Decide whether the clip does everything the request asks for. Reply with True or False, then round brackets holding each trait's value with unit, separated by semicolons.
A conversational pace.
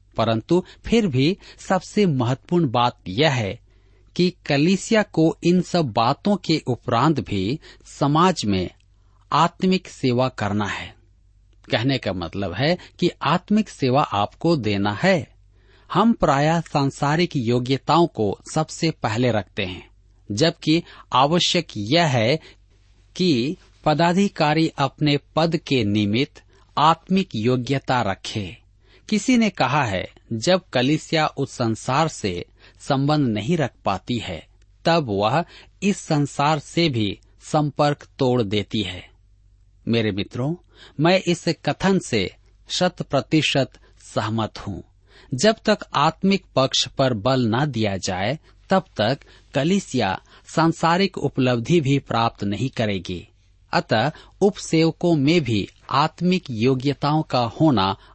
True (120 wpm)